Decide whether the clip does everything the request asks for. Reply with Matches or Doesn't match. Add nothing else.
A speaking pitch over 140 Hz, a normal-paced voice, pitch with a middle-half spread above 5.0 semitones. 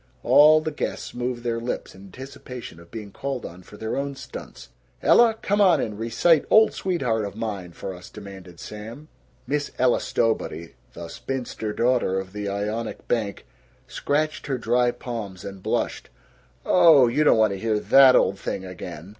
Doesn't match